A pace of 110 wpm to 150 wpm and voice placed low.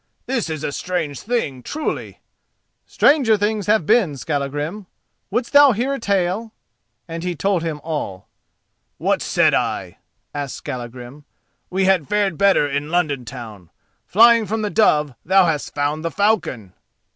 No: average, 145 wpm; medium, 175 Hz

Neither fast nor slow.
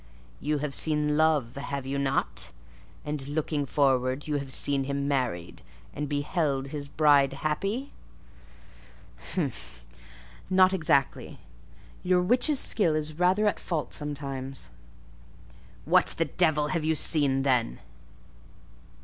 No: slow, 115 wpm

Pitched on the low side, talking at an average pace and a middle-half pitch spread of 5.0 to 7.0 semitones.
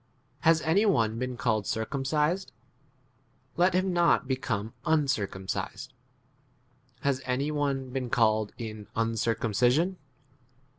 No: low, 130 Hz; slow, 105 wpm; wide, 5.4 semitones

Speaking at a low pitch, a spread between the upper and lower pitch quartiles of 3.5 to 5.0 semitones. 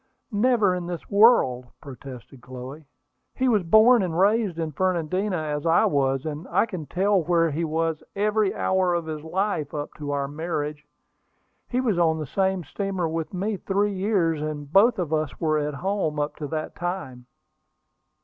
No: medium, 165 Hz; average, 4.6 semitones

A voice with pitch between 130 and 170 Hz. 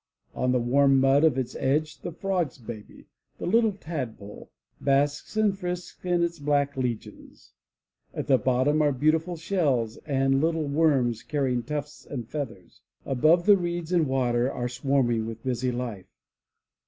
Yes: medium, 140 Hz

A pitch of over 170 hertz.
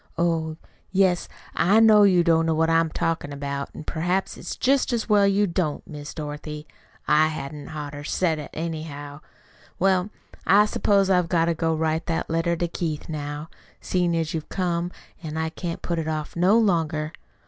No: medium, 165 Hz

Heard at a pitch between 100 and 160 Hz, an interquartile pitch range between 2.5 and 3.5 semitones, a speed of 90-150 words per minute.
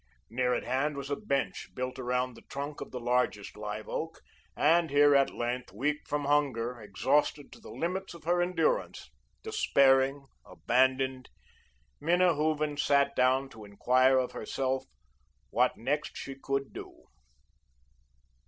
Yes: low, 135 Hz; average, 2.8 semitones; average, 145 wpm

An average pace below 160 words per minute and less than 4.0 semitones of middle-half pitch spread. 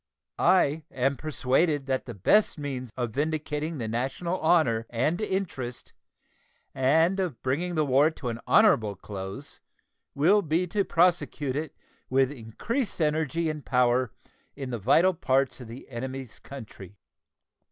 No: average, 140 wpm; average, 4.7 semitones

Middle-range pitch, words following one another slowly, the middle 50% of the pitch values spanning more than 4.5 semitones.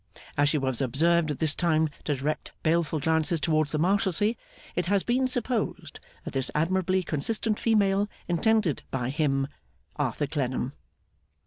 No: medium, 160 Hz; average, 145 wpm; average, 5.0 semitones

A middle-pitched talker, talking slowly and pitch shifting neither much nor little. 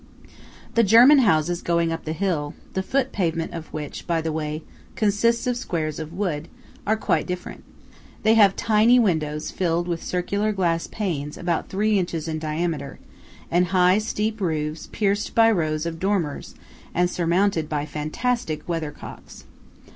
No: medium, 175 Hz; average, 150 wpm; average, 4.6 semitones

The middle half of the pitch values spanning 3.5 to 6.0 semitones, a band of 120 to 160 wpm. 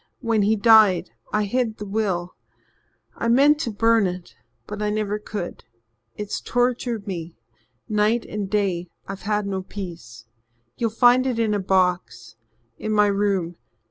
No: average, 3.1 semitones; average, 150 wpm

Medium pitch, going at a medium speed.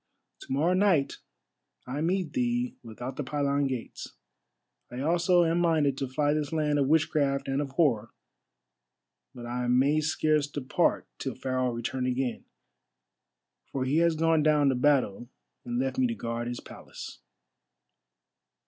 Yes: medium, 145 Hz; average, 150 wpm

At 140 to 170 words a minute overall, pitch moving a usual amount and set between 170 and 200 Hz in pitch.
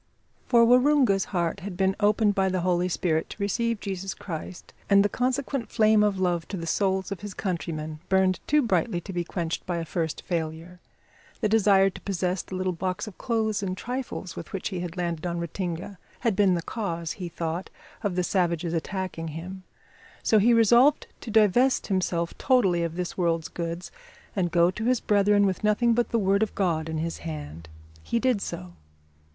No: average, 190 wpm; average, 3.6 semitones; high, 190 Hz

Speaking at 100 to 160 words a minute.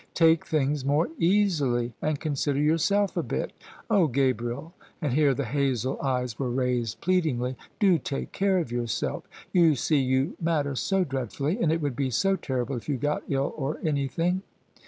No: average, 175 wpm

